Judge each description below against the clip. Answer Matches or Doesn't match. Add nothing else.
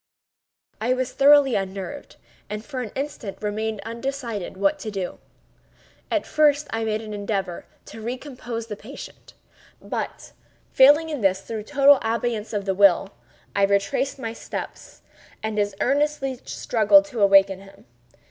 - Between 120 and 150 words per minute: Matches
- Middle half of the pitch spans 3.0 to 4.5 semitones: Doesn't match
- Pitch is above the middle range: Matches